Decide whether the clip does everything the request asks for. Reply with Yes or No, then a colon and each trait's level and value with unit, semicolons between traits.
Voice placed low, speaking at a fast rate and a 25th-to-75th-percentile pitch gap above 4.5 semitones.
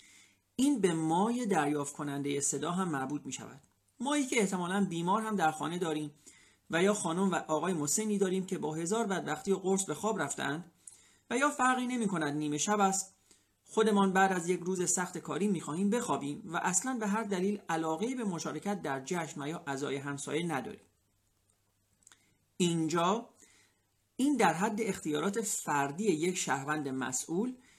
No: medium, 175 Hz; fast, 165 wpm; wide, 5.6 semitones